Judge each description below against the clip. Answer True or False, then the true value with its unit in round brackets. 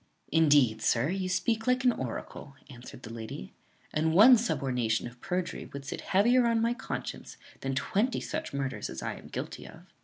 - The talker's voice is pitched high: False (160 Hz)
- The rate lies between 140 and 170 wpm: False (180 wpm)